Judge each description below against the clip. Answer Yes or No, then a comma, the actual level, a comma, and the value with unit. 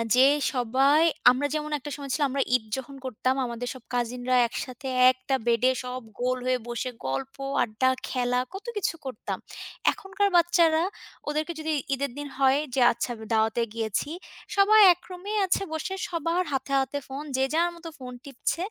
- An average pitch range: Yes, average, 4.2 semitones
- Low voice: No, very high, 270 Hz